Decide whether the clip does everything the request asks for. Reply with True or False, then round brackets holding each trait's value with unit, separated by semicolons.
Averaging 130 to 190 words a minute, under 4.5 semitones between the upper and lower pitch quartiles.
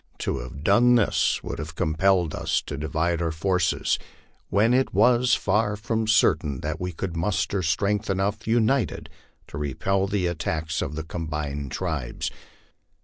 False (155 wpm; 4.9 semitones)